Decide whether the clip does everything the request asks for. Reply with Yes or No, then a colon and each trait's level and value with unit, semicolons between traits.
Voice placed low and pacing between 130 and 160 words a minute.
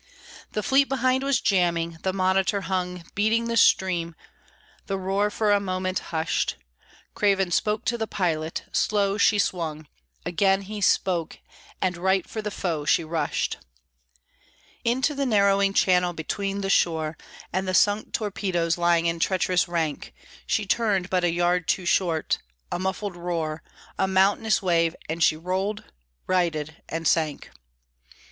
No: medium, 185 Hz; average, 145 wpm